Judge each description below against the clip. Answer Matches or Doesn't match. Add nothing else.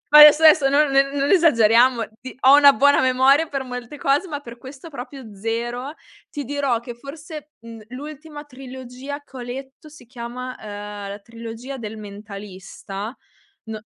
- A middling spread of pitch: Matches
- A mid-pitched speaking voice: Doesn't match